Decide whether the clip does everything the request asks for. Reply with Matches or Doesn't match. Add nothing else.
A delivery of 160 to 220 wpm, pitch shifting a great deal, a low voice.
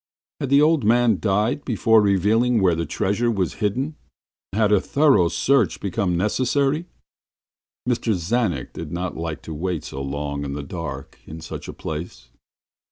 Matches